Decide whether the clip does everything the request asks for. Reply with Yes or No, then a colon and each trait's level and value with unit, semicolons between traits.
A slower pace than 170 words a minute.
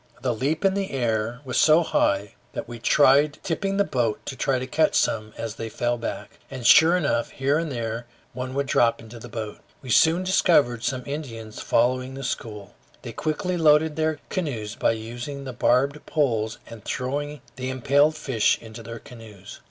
No: average, 180 wpm